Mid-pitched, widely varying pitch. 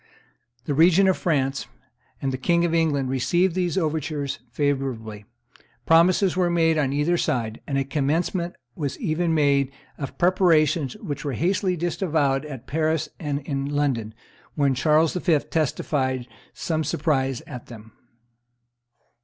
No: medium, 150 Hz; average, 3.7 semitones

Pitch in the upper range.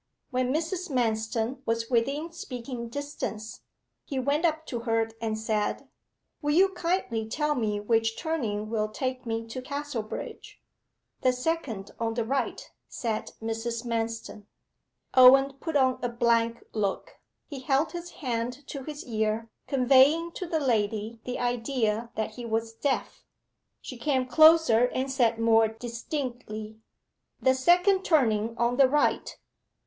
Yes: high, 245 Hz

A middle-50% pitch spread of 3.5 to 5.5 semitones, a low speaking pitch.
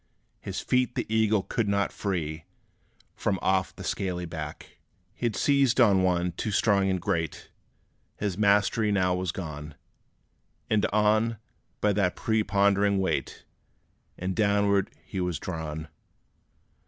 No: average, 2.7 semitones; low, 100 Hz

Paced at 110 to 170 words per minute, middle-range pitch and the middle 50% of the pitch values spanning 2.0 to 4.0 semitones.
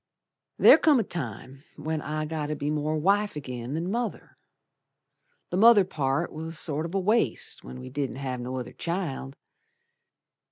No: average, 165 wpm; medium, 155 Hz; average, 4.9 semitones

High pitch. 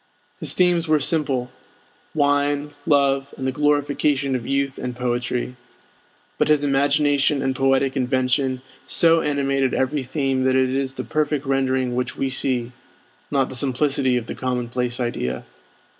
No: low, 135 Hz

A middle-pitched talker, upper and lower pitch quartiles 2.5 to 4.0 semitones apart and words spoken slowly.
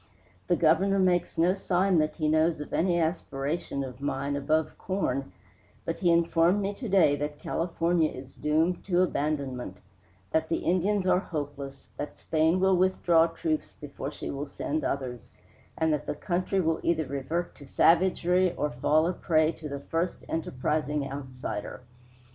No: medium, 160 Hz; average, 3.6 semitones; average, 160 wpm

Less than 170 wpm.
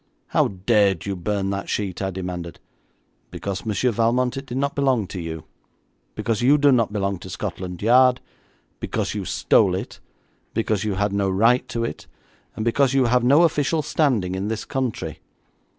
No: average, 175 wpm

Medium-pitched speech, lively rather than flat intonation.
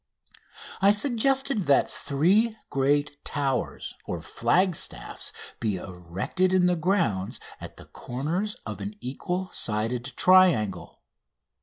Yes: medium, 155 Hz; wide, 8.1 semitones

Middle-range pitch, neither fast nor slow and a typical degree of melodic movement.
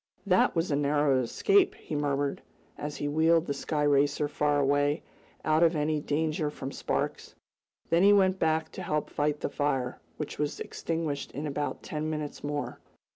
No: medium, 150 Hz; average, 175 wpm; narrow, 1.7 semitones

